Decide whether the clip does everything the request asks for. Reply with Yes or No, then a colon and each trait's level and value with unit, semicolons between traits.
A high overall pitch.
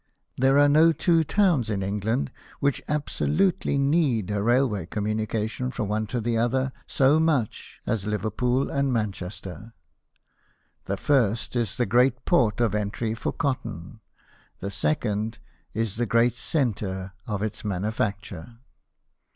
No: low, 115 Hz